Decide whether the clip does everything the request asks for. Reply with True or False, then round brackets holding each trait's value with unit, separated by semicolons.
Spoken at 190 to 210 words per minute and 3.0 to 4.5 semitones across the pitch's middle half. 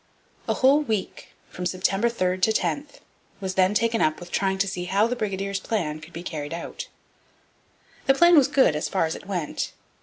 True (195 wpm; 4.2 semitones)